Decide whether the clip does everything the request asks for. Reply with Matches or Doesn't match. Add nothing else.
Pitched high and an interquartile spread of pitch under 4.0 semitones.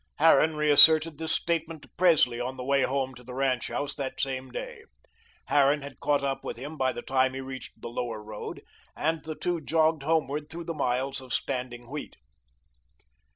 Doesn't match